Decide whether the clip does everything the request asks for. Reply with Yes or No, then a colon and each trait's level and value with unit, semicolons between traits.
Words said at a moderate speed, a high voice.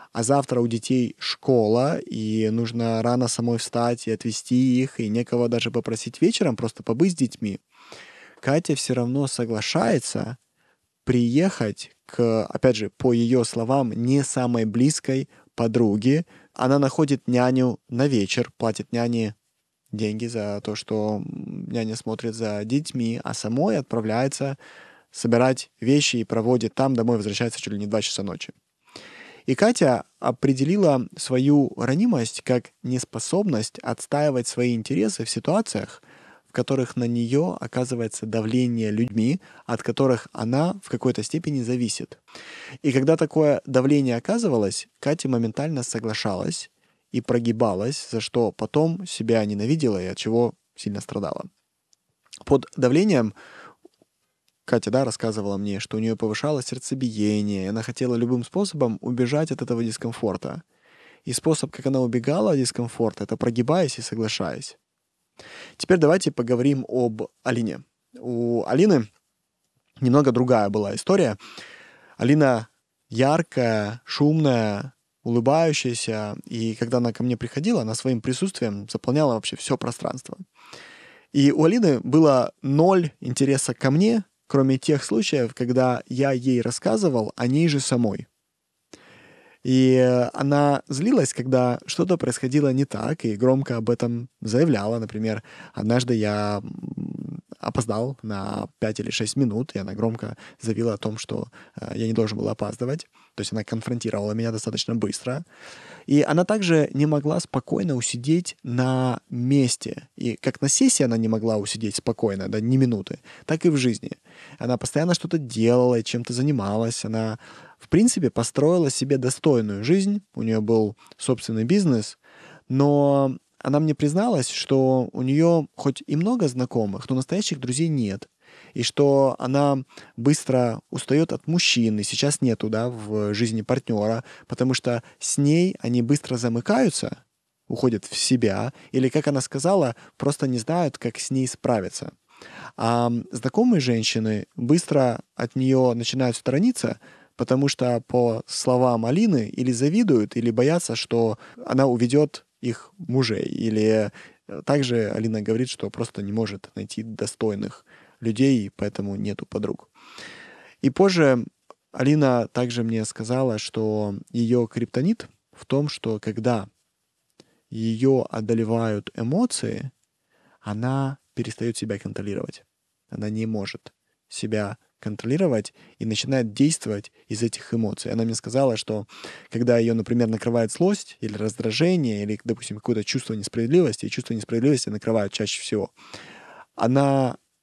No: average, 135 wpm; low, 120 Hz